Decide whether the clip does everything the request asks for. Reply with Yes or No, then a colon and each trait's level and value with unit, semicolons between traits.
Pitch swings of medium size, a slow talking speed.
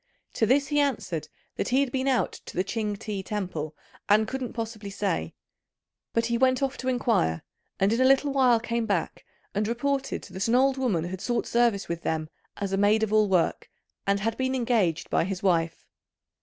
No: average, 4.8 semitones; average, 200 wpm